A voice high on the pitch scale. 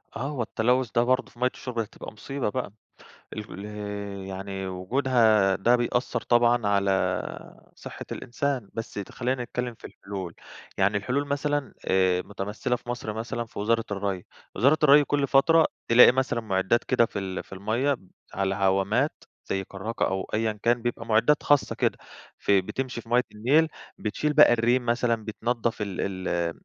No: low, 115 Hz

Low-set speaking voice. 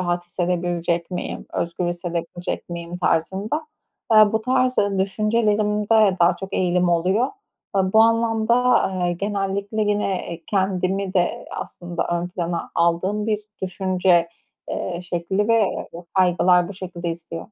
No: medium, 185 Hz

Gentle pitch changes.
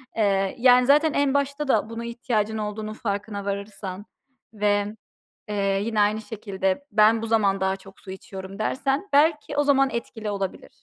No: average, 3.9 semitones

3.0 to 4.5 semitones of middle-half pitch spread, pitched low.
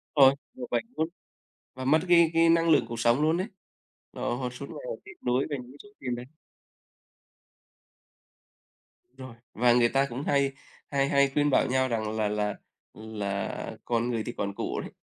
Yes: average, 3.8 semitones; low, 130 Hz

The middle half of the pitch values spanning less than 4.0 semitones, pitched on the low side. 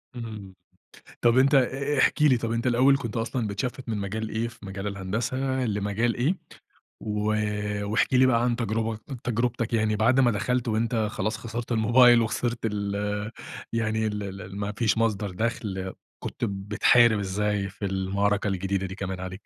Yes: average, 2.8 semitones; low, 110 Hz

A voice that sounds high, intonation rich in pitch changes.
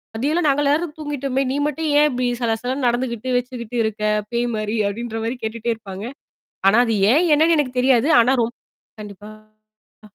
No: high, 245 Hz; average, 3.8 semitones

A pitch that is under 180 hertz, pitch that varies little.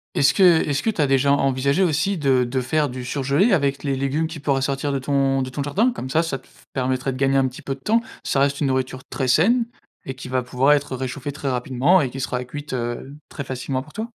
Yes: low, 135 Hz; narrow, 2.2 semitones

